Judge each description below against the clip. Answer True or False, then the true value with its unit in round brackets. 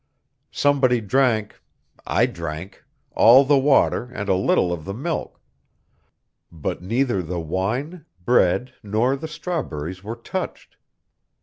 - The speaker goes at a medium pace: False (120 wpm)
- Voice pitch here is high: False (115 Hz)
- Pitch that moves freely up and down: True (6.7 semitones)